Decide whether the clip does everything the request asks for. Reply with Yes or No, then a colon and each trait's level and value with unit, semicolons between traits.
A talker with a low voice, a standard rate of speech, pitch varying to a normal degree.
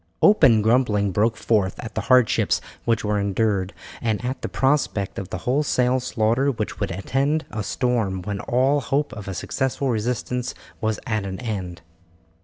Yes: low, 115 Hz; average, 165 wpm; average, 3.9 semitones